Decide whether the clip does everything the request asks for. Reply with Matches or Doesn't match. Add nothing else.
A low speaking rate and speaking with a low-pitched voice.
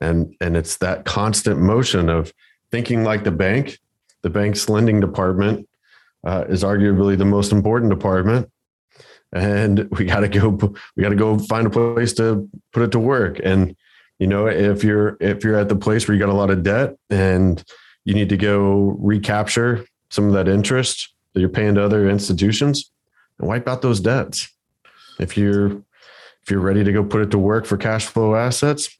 Doesn't match